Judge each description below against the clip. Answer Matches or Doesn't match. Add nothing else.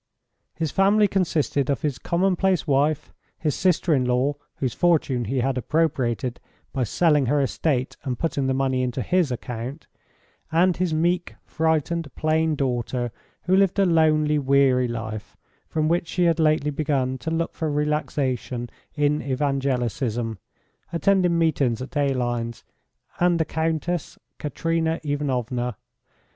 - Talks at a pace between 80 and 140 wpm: Matches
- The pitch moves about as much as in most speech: Matches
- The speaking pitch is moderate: Matches